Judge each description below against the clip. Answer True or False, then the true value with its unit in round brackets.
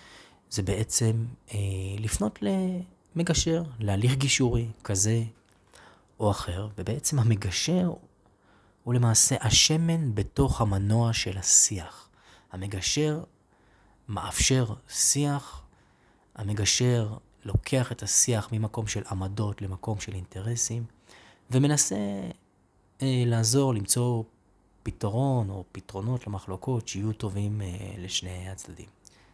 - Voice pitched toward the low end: True (110 Hz)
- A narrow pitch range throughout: False (4.0 semitones)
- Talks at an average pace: False (90 wpm)